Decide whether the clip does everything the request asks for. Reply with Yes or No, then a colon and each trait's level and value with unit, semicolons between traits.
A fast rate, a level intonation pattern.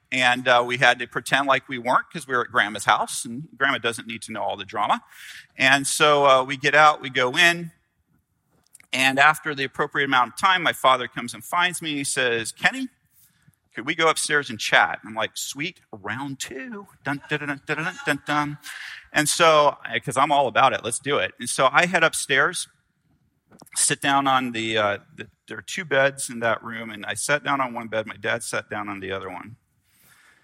No: fast, 220 wpm; average, 3.8 semitones